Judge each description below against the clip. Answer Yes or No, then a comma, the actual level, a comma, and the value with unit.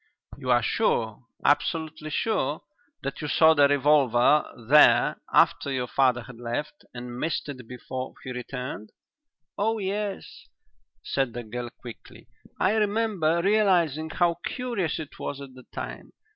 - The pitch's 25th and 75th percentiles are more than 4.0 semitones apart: Yes, average, 5.2 semitones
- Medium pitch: Yes, medium, 145 Hz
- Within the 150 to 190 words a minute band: No, average, 140 wpm